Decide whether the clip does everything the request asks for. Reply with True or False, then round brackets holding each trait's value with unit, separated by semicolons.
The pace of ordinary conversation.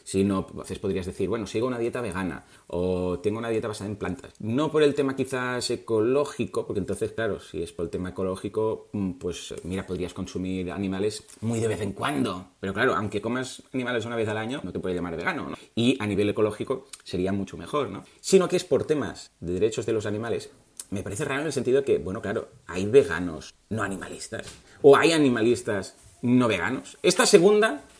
False (205 wpm)